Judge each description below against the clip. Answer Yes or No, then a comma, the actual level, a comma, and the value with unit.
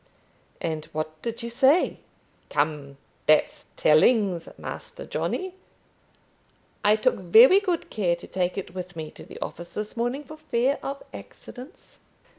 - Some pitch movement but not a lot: No, wide, 7.8 semitones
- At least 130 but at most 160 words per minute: Yes, average, 140 wpm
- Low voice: No, high, 210 Hz